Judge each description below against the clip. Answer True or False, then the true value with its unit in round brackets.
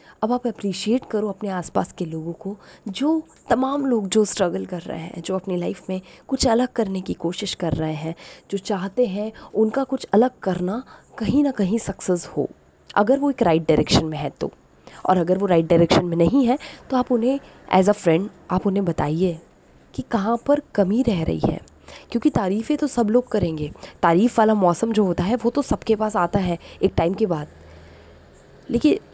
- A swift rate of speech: True (200 wpm)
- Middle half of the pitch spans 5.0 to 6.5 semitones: True (5.4 semitones)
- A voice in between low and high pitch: False (200 Hz)